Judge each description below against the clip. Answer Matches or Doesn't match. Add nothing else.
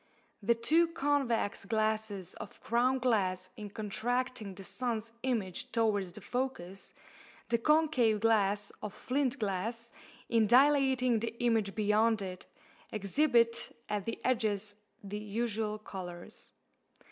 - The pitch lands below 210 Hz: Doesn't match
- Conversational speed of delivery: Doesn't match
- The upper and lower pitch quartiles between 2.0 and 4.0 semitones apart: Matches